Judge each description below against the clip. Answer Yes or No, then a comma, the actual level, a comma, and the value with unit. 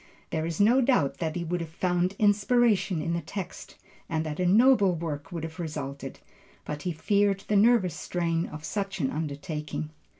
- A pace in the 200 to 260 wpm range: No, average, 180 wpm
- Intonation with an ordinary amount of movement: Yes, average, 4.2 semitones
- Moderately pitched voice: Yes, medium, 170 Hz